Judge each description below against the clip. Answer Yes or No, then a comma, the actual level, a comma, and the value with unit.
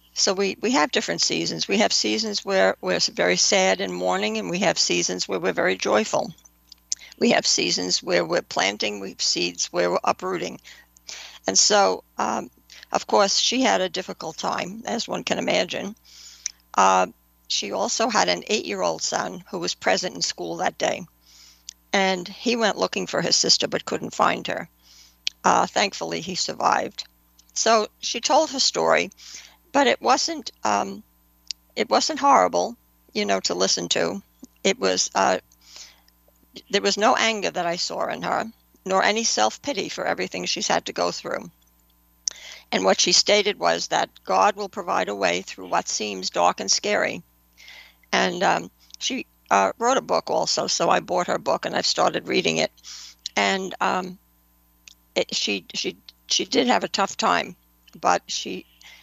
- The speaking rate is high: No, average, 170 wpm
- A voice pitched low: Yes, very low, 90 Hz